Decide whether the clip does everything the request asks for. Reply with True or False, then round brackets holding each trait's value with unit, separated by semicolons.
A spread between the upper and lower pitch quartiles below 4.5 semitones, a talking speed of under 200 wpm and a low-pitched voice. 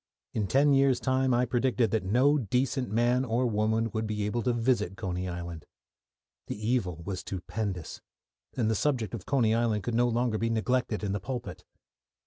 True (3.3 semitones; 180 wpm; 115 Hz)